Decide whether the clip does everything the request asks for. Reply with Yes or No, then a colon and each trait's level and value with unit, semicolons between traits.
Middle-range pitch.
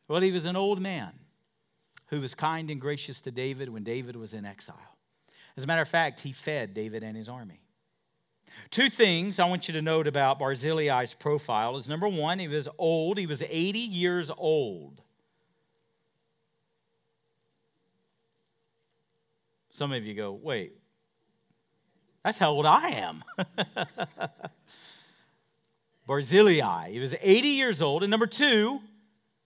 Yes: medium, 155 Hz